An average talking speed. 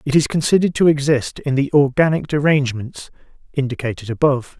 Yes: average, 145 wpm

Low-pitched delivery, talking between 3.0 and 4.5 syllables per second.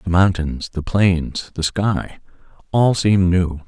Yes: very low, 90 Hz; 3.7 syllables/s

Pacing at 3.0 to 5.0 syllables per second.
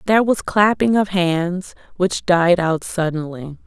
Yes: 4.0 syllables/s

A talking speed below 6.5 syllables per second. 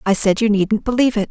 No: 7.6 syllables/s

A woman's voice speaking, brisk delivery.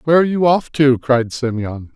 No: male; fast, 215 wpm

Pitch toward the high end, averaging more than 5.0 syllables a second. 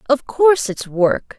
No: very high, 250 Hz; 4.2 syllables/s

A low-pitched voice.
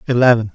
Yes: low, 120 Hz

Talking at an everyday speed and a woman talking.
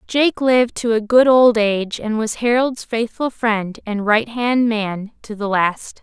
Yes: average, 180 wpm; female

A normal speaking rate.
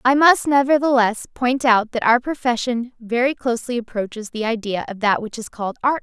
Yes: average, 190 wpm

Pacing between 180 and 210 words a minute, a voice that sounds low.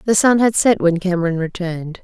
No: fast, 205 wpm; medium, 185 Hz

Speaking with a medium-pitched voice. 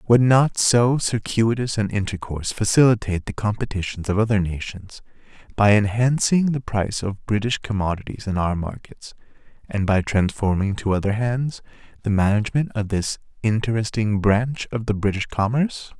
No: low, 105 Hz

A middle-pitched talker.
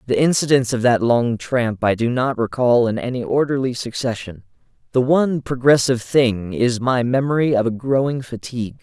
No: low, 125 Hz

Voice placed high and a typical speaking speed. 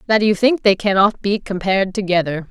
Yes: high, 200 Hz; average, 190 wpm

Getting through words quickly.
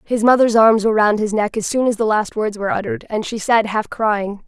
Yes: fast, 270 wpm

